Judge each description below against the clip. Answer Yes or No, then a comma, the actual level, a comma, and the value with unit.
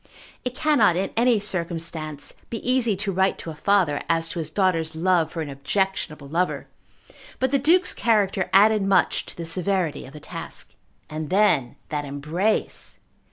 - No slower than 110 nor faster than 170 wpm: Yes, average, 165 wpm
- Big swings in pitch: No, average, 4.7 semitones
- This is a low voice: No, medium, 185 Hz